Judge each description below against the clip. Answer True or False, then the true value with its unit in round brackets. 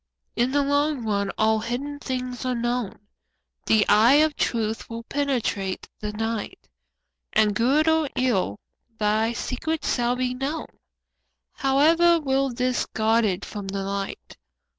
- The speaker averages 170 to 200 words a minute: False (135 wpm)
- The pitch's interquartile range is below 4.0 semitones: False (4.3 semitones)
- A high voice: True (245 Hz)